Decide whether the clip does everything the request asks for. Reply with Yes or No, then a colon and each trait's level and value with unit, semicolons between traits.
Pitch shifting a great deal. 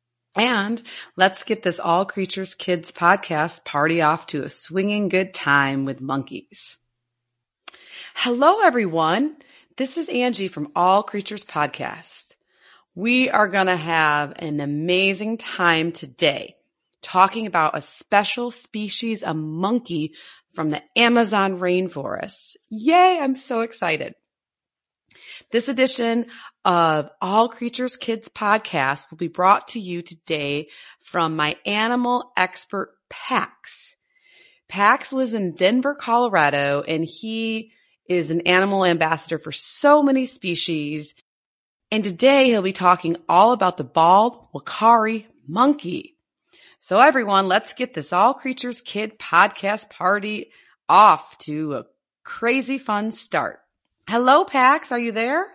Yes: wide, 6.6 semitones